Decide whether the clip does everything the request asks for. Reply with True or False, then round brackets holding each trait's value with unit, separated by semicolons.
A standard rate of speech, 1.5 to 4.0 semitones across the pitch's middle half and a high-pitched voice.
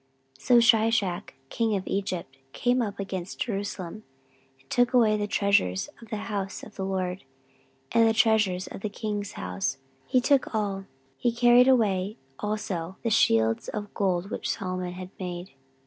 True (165 wpm; 3.4 semitones; 200 Hz)